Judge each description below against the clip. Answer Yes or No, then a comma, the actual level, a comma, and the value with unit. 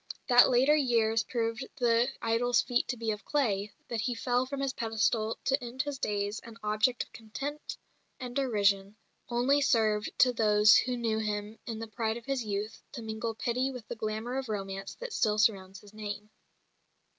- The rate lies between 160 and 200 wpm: Yes, average, 185 wpm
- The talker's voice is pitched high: Yes, high, 225 Hz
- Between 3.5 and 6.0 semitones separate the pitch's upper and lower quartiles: No, average, 2.7 semitones